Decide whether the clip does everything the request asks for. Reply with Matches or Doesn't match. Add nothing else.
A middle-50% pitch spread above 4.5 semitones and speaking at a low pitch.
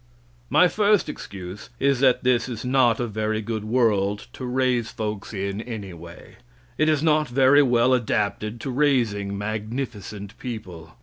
Doesn't match